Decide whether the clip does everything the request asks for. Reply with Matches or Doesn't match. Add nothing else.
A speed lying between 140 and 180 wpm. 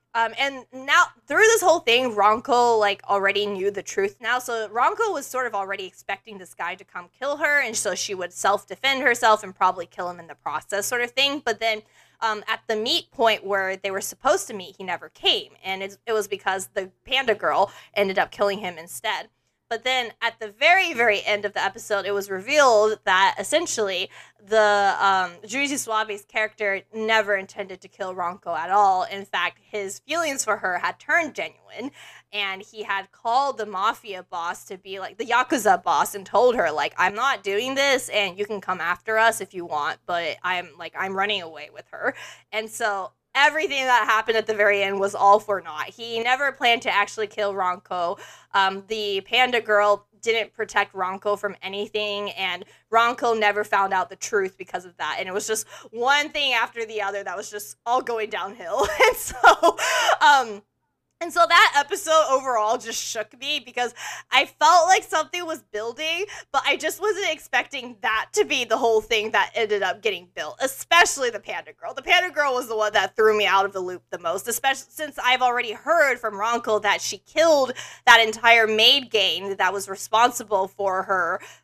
Doesn't match